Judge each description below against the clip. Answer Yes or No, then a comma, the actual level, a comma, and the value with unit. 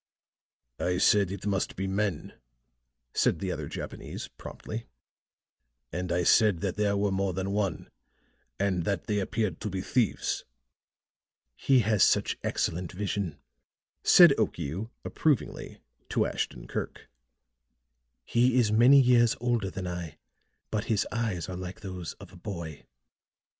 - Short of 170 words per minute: Yes, slow, 135 wpm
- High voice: No, low, 100 Hz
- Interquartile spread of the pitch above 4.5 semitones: No, average, 3.2 semitones